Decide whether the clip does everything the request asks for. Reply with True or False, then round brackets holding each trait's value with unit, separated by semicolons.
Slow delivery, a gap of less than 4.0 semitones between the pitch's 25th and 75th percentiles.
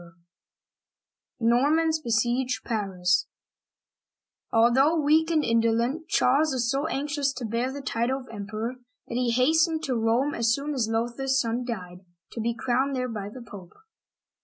False (155 wpm; 3.5 semitones)